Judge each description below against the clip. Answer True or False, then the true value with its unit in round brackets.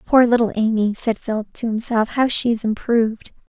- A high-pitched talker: True (230 Hz)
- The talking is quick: False (185 wpm)